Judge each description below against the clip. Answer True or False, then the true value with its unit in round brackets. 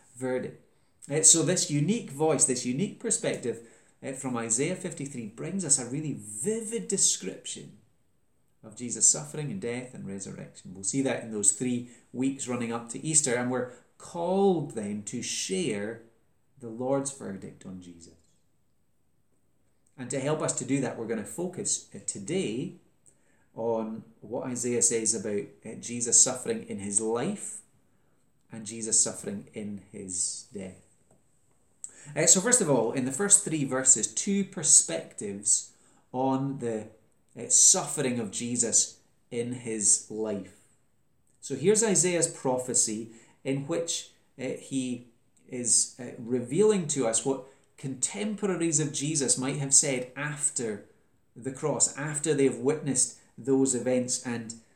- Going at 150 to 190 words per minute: False (135 wpm)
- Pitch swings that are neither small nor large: True (4.5 semitones)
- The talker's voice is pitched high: False (125 Hz)